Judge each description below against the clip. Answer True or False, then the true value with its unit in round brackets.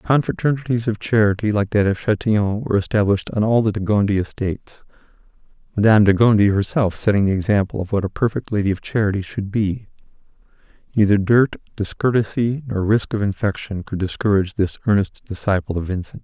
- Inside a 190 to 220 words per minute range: False (165 wpm)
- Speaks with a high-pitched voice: False (105 Hz)